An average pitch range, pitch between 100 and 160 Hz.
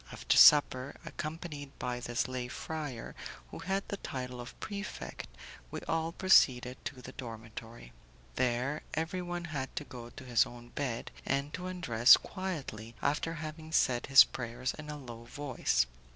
Yes: average, 4.7 semitones; low, 135 Hz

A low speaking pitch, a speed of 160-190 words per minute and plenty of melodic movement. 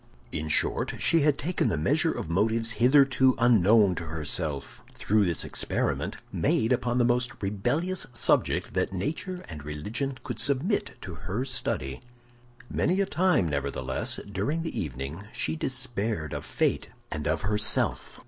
No: low, 110 Hz; average, 150 wpm; wide, 8.2 semitones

